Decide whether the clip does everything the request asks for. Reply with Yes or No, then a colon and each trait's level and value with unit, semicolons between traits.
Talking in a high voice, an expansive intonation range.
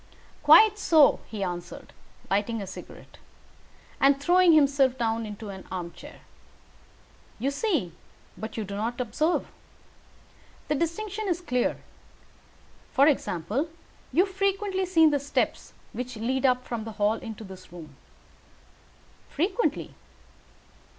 Yes: very high, 260 Hz; wide, 7.7 semitones